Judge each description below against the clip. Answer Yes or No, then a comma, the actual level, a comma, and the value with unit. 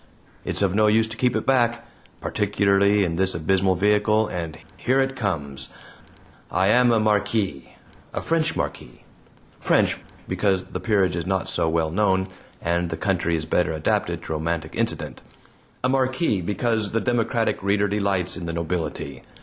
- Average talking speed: Yes, average, 160 wpm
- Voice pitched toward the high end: No, low, 100 Hz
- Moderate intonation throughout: Yes, average, 4.4 semitones